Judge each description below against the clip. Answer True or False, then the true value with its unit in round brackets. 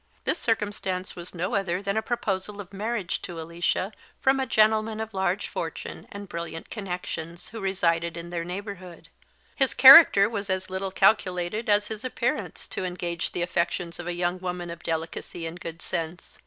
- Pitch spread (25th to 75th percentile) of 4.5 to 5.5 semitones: False (3.1 semitones)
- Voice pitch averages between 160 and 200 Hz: True (185 Hz)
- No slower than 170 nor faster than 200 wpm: True (175 wpm)